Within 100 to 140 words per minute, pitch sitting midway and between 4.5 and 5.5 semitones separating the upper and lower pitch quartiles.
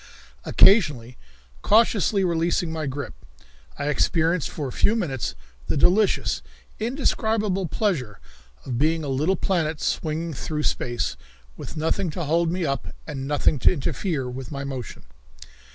Yes: slow, 135 wpm; medium, 160 Hz; average, 5.1 semitones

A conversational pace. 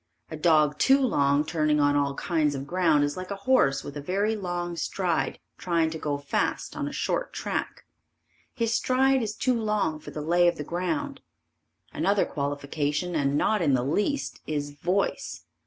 Yes: average, 180 wpm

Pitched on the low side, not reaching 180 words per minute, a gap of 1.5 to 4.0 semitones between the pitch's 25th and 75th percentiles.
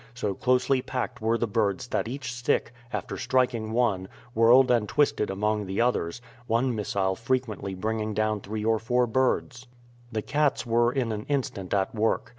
Yes: low, 115 Hz; average, 170 wpm; average, 2.9 semitones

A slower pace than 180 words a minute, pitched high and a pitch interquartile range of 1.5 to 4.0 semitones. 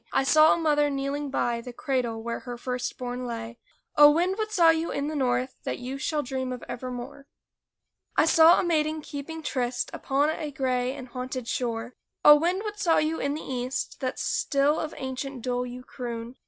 No: average, 195 wpm; very high, 270 Hz; average, 3.5 semitones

